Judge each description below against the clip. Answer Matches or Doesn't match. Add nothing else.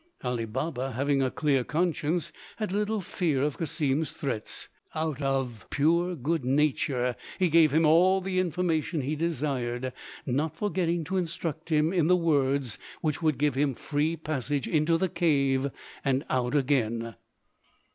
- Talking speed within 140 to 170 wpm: Matches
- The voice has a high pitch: Doesn't match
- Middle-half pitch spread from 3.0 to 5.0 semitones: Matches